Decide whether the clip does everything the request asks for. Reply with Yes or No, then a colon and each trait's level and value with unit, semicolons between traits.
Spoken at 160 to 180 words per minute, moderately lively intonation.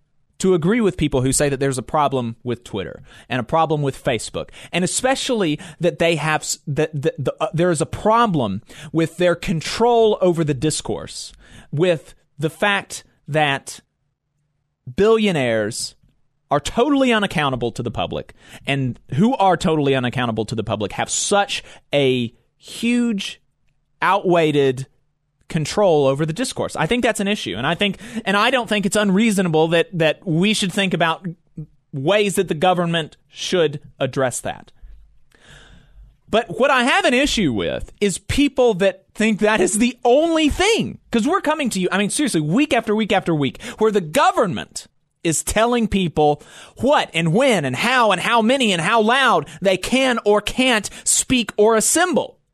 No: average, 165 wpm; wide, 6.7 semitones